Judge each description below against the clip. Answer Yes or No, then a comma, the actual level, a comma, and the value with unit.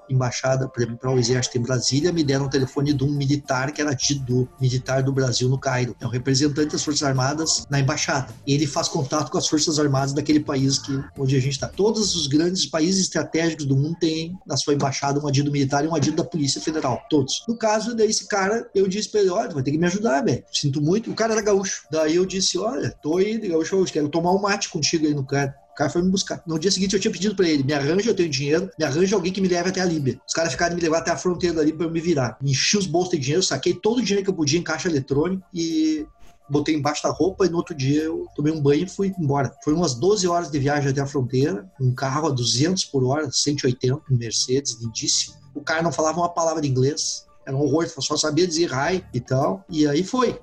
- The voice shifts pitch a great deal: No, average, 4.2 semitones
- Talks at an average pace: No, fast, 255 wpm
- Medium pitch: Yes, medium, 155 Hz